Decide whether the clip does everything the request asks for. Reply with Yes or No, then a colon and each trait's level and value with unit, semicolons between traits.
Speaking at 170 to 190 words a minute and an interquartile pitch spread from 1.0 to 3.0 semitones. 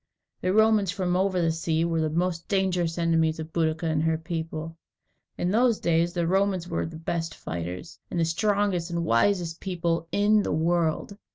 Yes: average, 180 wpm; narrow, 2.5 semitones